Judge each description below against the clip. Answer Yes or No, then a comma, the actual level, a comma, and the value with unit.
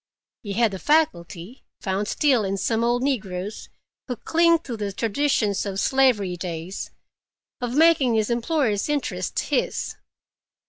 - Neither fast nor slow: No, slow, 125 wpm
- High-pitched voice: Yes, high, 230 Hz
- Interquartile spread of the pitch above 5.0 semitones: Yes, wide, 5.4 semitones